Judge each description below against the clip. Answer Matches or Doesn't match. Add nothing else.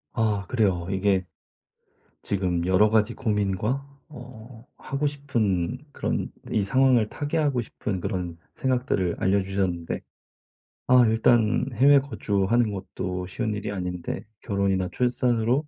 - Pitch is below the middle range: Matches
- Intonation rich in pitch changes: Doesn't match